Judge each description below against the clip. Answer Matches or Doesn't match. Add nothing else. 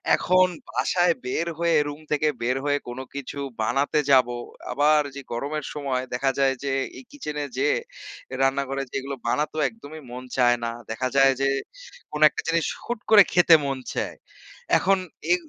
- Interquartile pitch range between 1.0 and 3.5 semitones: Matches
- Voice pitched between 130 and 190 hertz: Matches